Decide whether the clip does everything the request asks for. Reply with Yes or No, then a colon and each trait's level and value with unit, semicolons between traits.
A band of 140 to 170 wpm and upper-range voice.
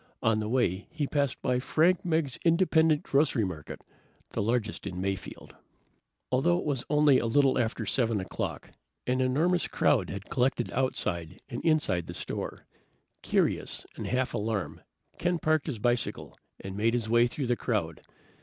No: average, 160 wpm; low, 125 Hz